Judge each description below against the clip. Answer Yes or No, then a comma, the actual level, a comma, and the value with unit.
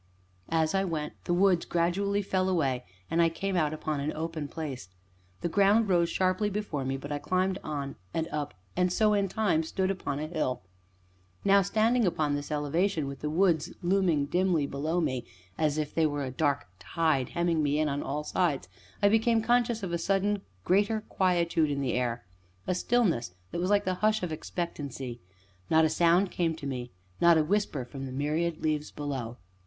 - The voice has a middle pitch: Yes, medium, 165 Hz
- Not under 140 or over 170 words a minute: No, average, 190 wpm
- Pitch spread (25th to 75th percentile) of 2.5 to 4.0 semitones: No, average, 4.5 semitones